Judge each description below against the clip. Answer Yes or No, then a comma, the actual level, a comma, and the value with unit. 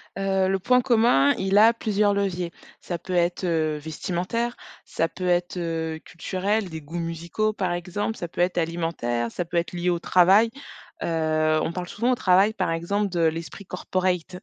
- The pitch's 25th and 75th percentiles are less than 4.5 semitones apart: Yes, average, 2.9 semitones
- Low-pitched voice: No, medium, 180 Hz